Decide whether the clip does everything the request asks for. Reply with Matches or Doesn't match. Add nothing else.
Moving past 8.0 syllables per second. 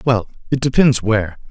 Doesn't match